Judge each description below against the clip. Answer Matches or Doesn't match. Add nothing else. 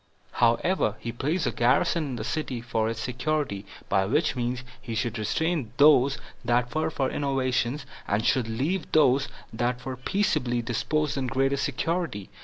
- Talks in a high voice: Doesn't match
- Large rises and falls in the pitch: Doesn't match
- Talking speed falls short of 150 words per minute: Doesn't match